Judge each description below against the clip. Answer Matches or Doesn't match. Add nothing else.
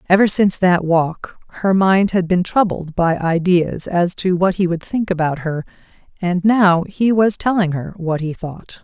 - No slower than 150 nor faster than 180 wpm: Doesn't match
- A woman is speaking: Matches